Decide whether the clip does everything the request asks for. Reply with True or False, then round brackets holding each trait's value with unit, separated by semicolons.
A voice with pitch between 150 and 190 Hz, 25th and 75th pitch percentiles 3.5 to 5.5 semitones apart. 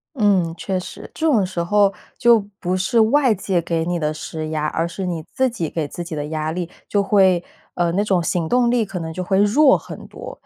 True (185 Hz; 3.9 semitones)